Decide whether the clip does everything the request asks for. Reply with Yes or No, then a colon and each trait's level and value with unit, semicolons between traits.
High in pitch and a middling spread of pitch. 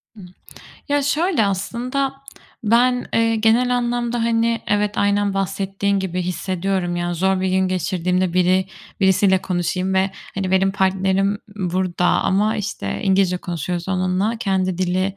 Yes: high, 195 Hz; average, 3.0 semitones